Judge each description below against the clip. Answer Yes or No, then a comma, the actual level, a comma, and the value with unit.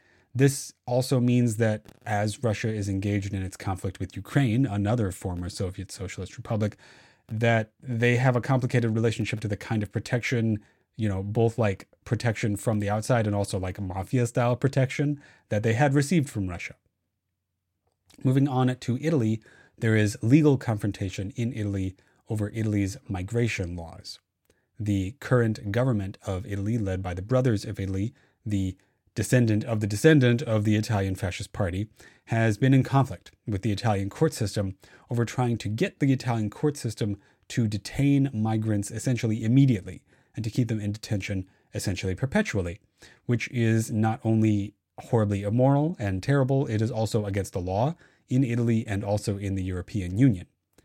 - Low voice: Yes, low, 110 Hz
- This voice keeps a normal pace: Yes, average, 160 wpm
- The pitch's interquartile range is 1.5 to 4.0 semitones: Yes, average, 3.7 semitones